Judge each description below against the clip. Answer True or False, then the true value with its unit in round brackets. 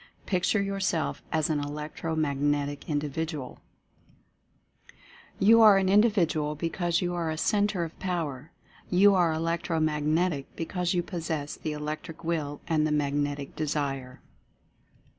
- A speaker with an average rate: False (130 wpm)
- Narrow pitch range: False (3.1 semitones)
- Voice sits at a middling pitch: True (160 Hz)